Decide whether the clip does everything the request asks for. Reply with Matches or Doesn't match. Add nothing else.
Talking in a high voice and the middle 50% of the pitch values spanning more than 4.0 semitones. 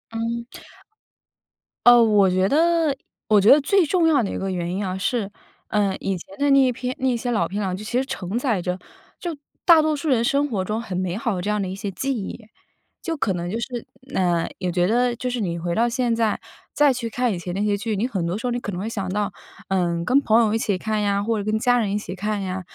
Matches